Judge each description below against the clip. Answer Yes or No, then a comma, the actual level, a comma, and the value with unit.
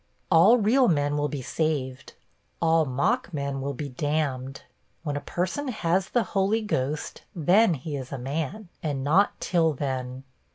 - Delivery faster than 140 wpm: Yes, average, 160 wpm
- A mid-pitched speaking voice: Yes, medium, 155 Hz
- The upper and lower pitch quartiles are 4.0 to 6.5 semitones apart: Yes, wide, 5.4 semitones